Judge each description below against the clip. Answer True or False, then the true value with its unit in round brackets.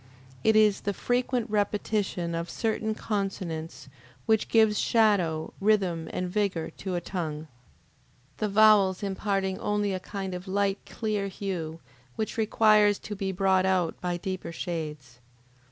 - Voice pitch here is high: True (195 Hz)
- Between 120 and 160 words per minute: True (135 wpm)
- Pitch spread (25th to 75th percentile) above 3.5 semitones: False (3.1 semitones)